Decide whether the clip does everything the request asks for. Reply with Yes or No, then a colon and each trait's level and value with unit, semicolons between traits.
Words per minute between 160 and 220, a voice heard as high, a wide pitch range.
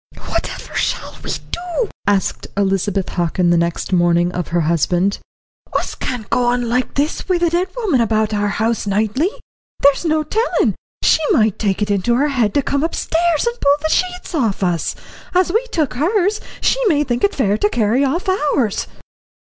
Yes: average, 180 wpm; high, 245 Hz; wide, 8.4 semitones